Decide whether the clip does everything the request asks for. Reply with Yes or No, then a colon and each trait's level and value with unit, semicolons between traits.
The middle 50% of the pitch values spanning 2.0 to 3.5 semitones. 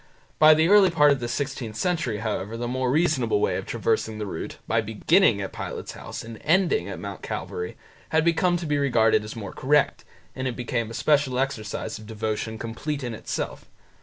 No: wide, 5.6 semitones